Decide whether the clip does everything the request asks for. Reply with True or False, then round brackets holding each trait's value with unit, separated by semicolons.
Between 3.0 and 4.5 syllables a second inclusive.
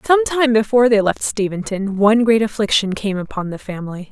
False (5.7 syllables/s)